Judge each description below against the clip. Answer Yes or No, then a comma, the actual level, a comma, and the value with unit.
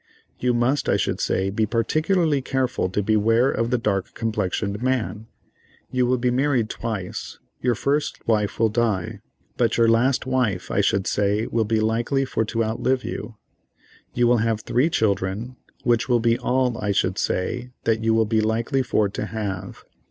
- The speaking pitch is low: Yes, low, 115 Hz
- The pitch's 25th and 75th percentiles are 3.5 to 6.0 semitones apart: No, average, 2.8 semitones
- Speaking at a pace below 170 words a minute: No, average, 175 wpm